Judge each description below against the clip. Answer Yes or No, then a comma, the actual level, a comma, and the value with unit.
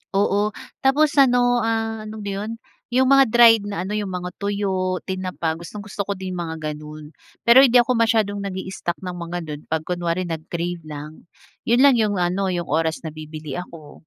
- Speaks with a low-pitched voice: No, high, 190 Hz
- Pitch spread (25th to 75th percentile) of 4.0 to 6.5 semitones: Yes, average, 4.7 semitones